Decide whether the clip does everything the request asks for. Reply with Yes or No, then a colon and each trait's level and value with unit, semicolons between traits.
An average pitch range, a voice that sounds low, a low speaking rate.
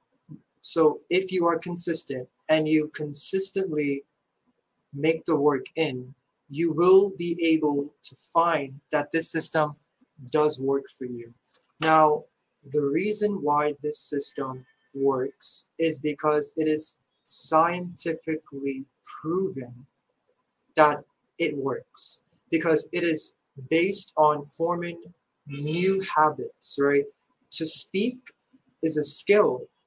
No: average, 3.0 semitones; medium, 155 Hz; slow, 110 wpm